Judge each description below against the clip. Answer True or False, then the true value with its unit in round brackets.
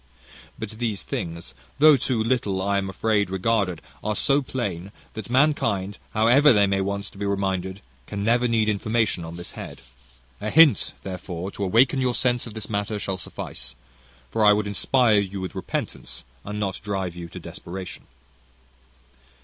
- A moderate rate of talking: True (165 wpm)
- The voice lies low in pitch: True (100 Hz)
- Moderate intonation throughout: True (3.3 semitones)